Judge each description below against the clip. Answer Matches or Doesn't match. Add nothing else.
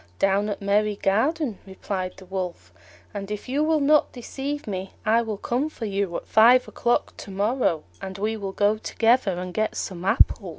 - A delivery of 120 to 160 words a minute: Doesn't match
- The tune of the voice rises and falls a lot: Doesn't match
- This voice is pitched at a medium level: Doesn't match